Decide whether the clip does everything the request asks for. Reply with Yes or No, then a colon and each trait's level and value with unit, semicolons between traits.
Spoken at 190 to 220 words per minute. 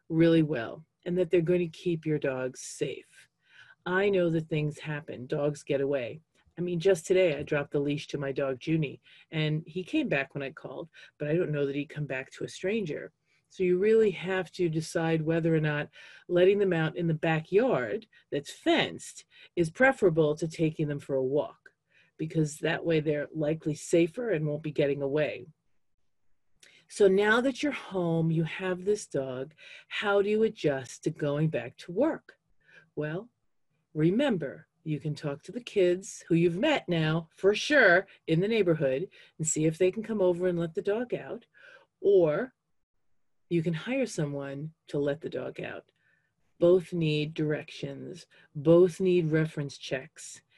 No: average, 175 wpm